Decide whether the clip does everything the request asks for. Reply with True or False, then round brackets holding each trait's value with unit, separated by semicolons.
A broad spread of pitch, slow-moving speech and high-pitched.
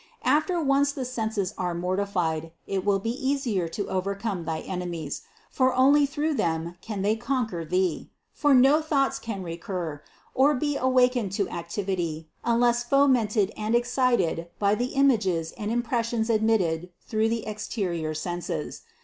False (6.0 semitones; 150 wpm; 215 Hz)